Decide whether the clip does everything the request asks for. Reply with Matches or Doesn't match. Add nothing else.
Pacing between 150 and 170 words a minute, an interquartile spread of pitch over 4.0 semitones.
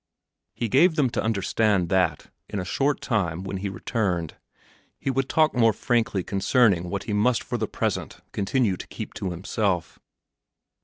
Matches